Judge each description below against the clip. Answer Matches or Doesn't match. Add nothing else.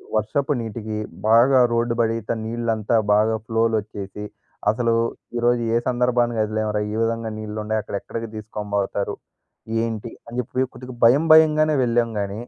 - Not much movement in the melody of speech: Matches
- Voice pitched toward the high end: Doesn't match